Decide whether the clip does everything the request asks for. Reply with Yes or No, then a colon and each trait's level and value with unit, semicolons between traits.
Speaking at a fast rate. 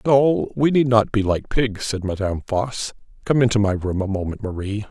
Yes: fast, 210 wpm